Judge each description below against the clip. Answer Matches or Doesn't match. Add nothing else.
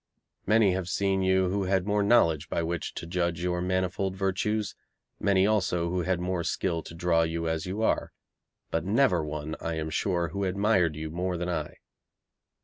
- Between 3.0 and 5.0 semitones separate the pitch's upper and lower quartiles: Doesn't match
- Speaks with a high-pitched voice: Doesn't match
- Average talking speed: Matches